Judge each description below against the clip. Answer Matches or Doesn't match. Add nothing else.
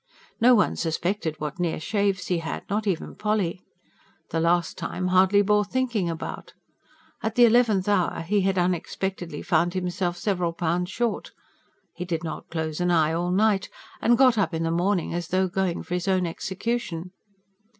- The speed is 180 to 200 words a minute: Doesn't match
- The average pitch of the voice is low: Doesn't match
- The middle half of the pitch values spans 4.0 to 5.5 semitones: Doesn't match